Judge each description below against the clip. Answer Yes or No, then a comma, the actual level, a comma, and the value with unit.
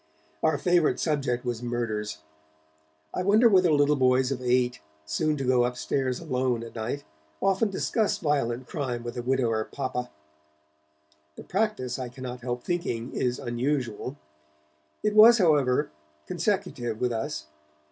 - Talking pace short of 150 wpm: Yes, slow, 135 wpm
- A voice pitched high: No, low, 130 Hz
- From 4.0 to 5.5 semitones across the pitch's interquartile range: No, average, 3.6 semitones